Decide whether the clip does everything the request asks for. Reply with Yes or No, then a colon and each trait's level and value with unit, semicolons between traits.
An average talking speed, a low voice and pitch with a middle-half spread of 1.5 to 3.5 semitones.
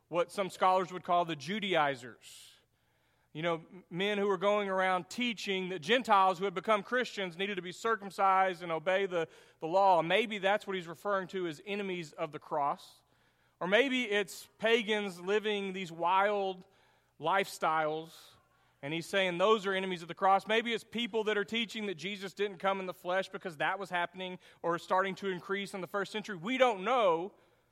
No: average, 190 wpm; high, 190 Hz; narrow, 2.5 semitones